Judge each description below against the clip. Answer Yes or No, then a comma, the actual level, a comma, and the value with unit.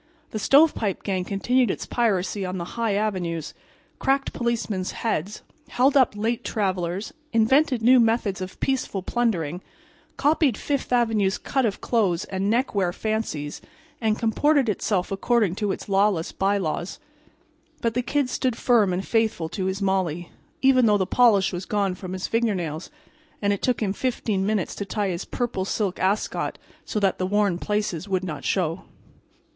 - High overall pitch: Yes, high, 205 Hz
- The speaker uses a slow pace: No, average, 160 wpm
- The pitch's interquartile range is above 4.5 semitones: No, average, 3.9 semitones